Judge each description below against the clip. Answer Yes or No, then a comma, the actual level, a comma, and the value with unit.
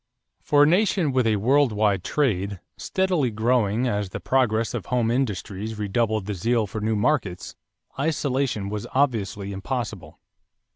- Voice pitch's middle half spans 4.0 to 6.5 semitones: Yes, average, 4.5 semitones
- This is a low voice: Yes, low, 110 Hz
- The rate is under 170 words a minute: Yes, average, 150 wpm